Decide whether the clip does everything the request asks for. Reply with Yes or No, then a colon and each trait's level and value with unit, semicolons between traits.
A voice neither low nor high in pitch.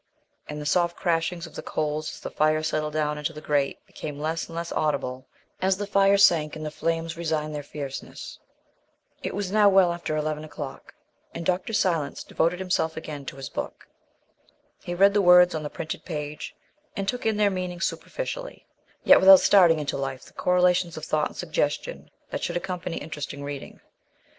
Yes: medium, 165 Hz